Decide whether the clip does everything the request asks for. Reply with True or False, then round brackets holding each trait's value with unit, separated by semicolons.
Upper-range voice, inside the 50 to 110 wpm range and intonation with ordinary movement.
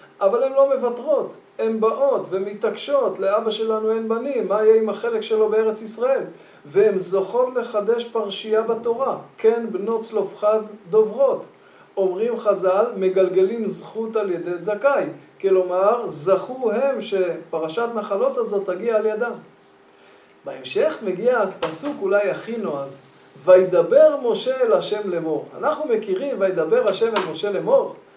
False (220 Hz; 130 wpm; 4.3 semitones)